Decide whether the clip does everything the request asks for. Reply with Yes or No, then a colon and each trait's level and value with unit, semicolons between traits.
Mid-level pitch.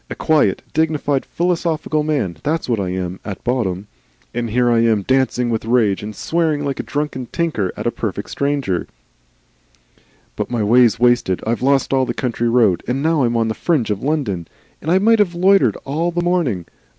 No: low, 125 Hz